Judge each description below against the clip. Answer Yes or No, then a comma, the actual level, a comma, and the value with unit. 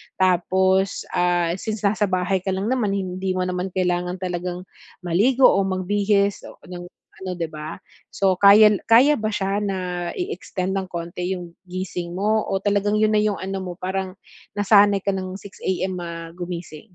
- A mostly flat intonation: Yes, narrow, 2.2 semitones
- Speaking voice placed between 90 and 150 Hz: No, high, 190 Hz